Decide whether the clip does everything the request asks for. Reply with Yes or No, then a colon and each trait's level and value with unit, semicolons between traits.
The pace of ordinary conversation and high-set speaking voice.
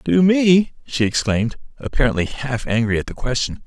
No: average, 165 wpm; low, 135 Hz